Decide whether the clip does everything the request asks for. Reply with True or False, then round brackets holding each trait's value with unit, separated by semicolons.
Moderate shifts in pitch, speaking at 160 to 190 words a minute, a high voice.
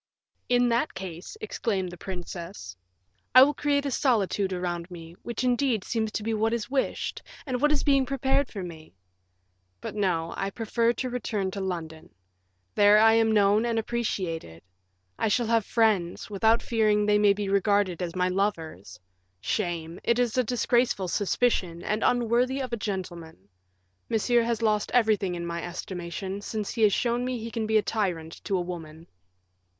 True (4.7 semitones; 170 wpm; 210 Hz)